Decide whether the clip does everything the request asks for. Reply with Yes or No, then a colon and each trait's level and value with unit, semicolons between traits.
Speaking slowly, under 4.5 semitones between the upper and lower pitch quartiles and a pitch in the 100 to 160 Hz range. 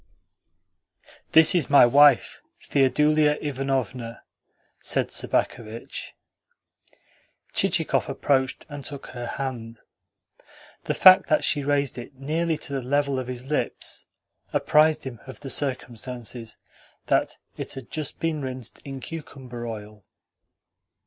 Yes: slow, 115 wpm; average, 3.0 semitones; low, 135 Hz